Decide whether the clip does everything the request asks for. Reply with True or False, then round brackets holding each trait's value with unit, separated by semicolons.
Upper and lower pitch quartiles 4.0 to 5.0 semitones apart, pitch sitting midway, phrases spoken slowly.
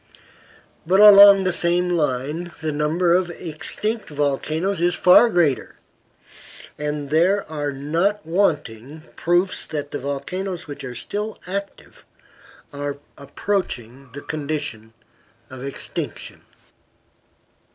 True (4.3 semitones; 160 Hz; 110 wpm)